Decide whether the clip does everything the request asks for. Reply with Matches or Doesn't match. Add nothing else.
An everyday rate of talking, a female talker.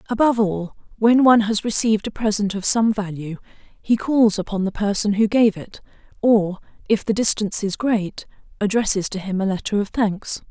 Matches